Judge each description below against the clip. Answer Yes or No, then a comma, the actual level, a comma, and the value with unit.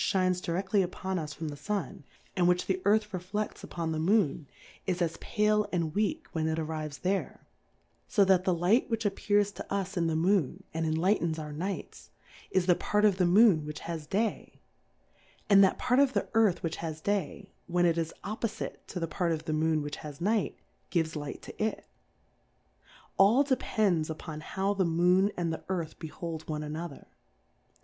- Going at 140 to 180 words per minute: No, average, 195 wpm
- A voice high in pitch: No, medium, 180 Hz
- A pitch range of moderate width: Yes, average, 3.9 semitones